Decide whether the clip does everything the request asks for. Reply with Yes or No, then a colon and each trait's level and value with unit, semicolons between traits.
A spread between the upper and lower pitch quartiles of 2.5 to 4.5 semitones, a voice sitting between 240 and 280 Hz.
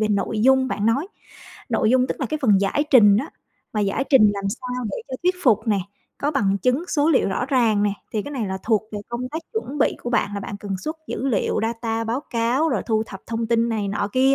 No: average, 4.1 semitones; high, 230 Hz